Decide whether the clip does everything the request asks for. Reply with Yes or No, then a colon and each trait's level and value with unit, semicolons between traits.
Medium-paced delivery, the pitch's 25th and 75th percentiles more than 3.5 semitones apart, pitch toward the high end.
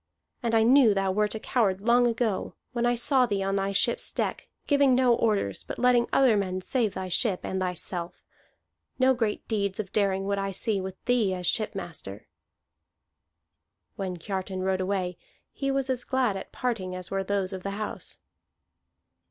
Yes: average, 175 wpm; average, 4.1 semitones; high, 200 Hz